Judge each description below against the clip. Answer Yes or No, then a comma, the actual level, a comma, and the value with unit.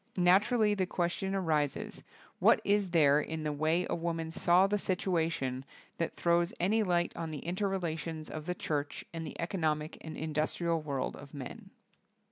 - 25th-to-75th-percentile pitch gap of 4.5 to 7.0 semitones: No, average, 2.8 semitones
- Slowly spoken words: No, average, 170 wpm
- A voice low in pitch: No, medium, 165 Hz